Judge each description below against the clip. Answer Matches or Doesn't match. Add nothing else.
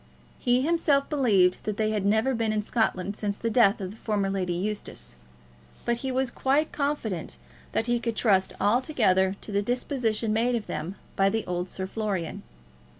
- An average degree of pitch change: Matches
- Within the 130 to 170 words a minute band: Doesn't match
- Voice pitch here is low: Doesn't match